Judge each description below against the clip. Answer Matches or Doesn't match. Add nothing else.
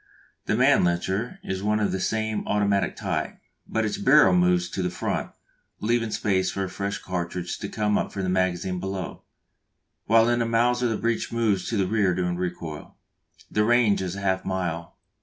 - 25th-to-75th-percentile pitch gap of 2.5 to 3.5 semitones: Matches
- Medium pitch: Doesn't match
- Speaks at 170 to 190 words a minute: Matches